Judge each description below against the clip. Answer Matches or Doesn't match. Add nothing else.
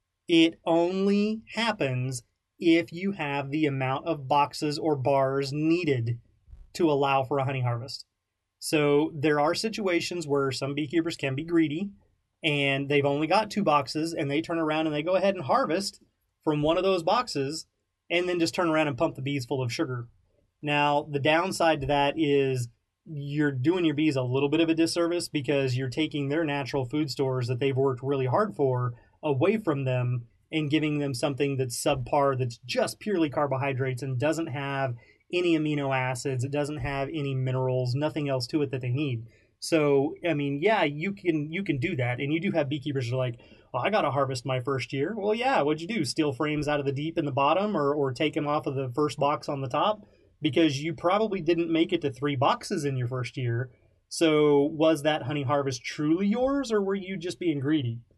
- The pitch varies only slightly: Doesn't match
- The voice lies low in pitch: Doesn't match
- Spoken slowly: Doesn't match